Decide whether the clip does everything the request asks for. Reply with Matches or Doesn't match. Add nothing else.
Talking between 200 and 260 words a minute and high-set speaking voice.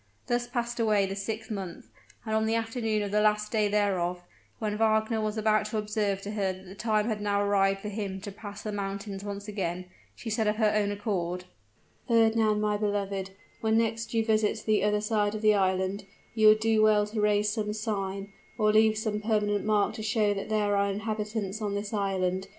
Matches